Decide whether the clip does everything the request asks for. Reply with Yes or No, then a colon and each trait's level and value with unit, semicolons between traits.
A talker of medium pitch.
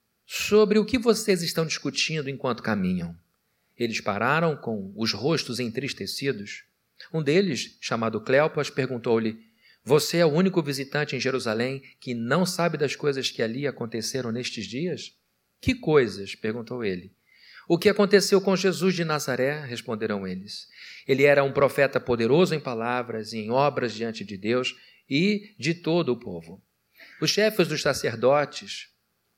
No: low, 130 Hz